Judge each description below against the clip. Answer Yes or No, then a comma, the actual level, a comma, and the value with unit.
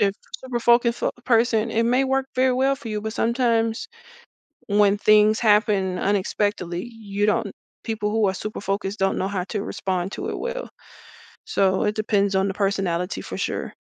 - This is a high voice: Yes, high, 210 Hz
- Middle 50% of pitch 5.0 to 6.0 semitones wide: No, average, 2.8 semitones